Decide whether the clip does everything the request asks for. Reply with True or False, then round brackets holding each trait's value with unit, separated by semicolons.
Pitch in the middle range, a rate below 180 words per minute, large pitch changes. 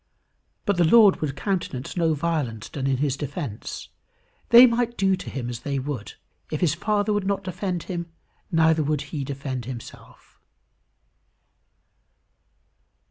True (160 Hz; 140 wpm; 5.8 semitones)